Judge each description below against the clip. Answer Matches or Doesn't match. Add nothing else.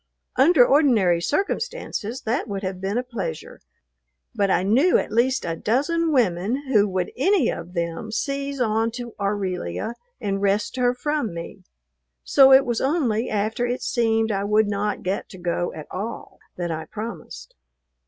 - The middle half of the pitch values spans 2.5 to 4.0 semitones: Doesn't match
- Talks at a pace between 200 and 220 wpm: Doesn't match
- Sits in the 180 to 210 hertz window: Doesn't match